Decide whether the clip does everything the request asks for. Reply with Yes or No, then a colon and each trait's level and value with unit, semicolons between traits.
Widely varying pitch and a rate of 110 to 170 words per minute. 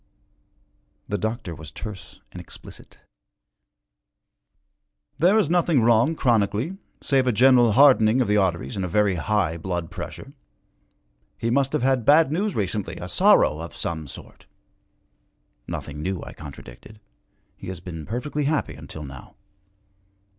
Yes: wide, 7.6 semitones; average, 140 wpm